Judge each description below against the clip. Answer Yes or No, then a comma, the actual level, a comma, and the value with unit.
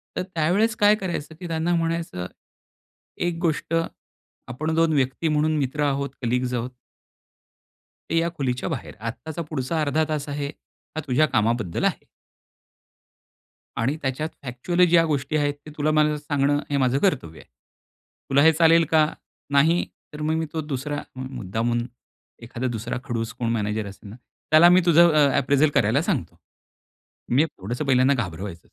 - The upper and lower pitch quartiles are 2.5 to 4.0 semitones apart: No, average, 4.4 semitones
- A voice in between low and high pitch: Yes, medium, 145 Hz